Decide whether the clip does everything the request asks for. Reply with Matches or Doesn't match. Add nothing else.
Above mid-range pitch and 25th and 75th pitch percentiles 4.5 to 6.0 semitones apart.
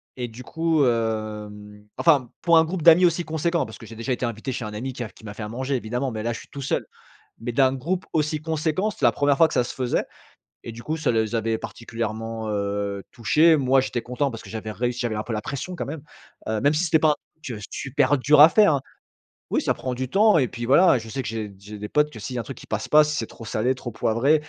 Doesn't match